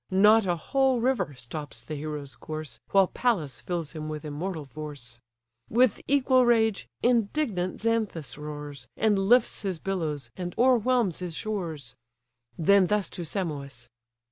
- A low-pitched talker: No, medium, 180 Hz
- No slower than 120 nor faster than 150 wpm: Yes, average, 140 wpm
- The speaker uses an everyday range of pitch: No, wide, 6.8 semitones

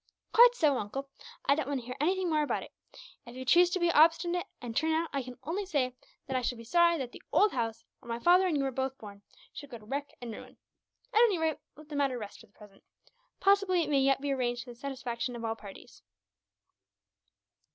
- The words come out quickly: Yes, fast, 235 wpm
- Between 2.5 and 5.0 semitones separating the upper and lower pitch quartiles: No, wide, 5.5 semitones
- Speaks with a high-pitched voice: Yes, very high, 275 Hz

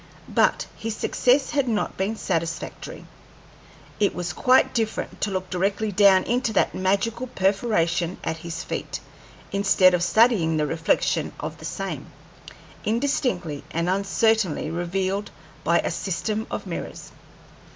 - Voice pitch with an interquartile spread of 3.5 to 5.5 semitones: Yes, average, 4.1 semitones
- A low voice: No, high, 195 Hz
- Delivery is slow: Yes, slow, 130 wpm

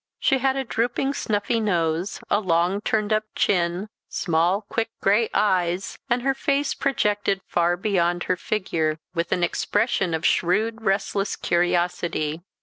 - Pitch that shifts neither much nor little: Yes, average, 4.1 semitones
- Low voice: No, high, 195 Hz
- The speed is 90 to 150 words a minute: Yes, average, 145 wpm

